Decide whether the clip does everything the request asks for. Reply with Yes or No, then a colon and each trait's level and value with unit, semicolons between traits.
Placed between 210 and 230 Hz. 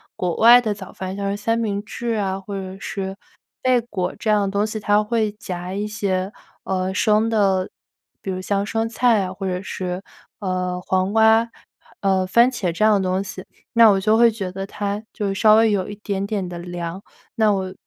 No: high, 200 Hz